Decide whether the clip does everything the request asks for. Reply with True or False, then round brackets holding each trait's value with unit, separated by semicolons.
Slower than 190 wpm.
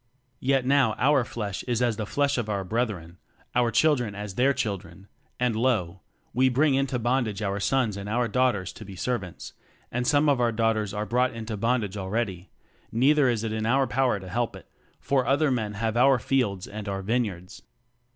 False (200 wpm)